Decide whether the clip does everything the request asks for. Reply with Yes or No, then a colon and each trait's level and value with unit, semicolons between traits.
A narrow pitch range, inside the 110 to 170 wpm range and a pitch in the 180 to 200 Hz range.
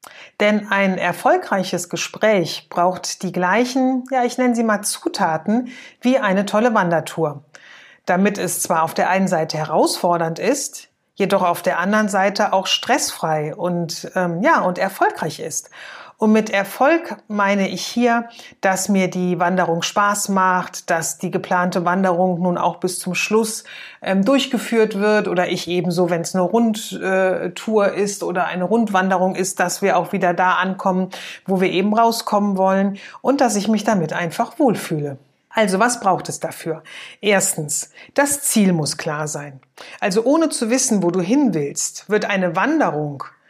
No: average, 3.7 semitones; average, 160 wpm; high, 190 Hz